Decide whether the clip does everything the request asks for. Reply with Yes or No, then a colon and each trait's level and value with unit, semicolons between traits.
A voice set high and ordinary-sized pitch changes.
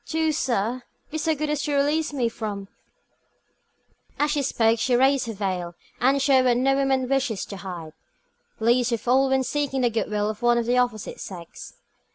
Yes: very high, 250 Hz; average, 3.8 semitones